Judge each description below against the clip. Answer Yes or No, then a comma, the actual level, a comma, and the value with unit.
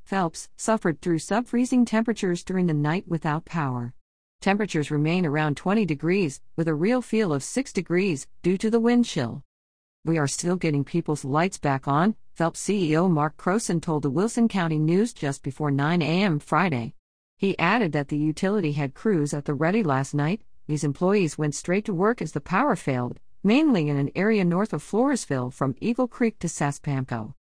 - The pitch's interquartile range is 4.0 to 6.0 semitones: Yes, wide, 5.4 semitones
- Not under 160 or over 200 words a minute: Yes, average, 185 wpm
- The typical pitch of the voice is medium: Yes, medium, 165 Hz